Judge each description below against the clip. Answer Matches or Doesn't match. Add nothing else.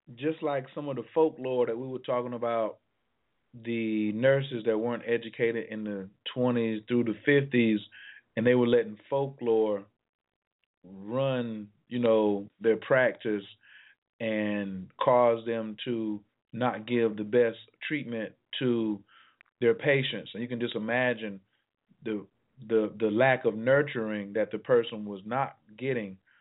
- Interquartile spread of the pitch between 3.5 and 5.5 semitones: Doesn't match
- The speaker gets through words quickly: Doesn't match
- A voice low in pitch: Matches